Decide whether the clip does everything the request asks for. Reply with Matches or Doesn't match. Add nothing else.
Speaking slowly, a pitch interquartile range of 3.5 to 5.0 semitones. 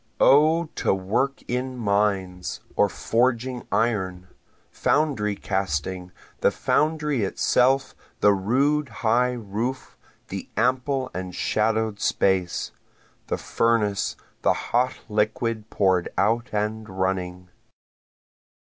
Matches